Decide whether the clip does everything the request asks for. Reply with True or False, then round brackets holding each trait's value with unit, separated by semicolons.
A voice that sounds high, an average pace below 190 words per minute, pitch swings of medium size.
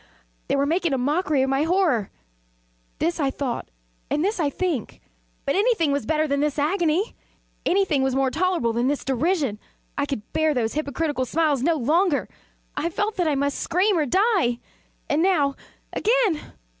True (305 Hz; 170 wpm; 4.5 semitones)